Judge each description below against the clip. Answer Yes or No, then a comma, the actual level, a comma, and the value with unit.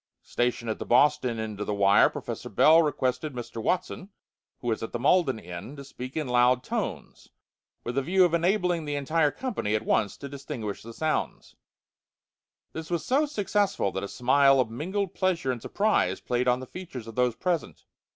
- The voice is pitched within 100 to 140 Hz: Yes, low, 135 Hz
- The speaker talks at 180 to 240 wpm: Yes, average, 190 wpm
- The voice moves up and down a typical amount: No, wide, 5.9 semitones